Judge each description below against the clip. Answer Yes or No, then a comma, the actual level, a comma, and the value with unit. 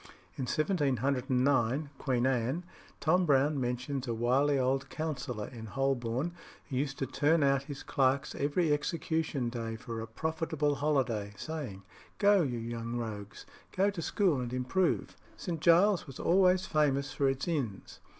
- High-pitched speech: No, low, 135 Hz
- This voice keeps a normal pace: Yes, average, 150 wpm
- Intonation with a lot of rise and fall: No, average, 4.1 semitones